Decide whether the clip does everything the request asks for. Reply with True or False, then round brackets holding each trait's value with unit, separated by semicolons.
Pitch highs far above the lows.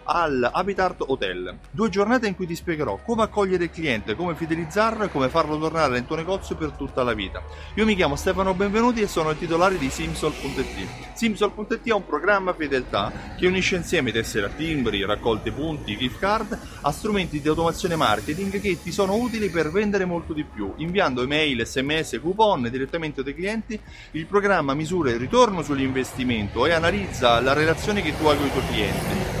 True (6.8 semitones)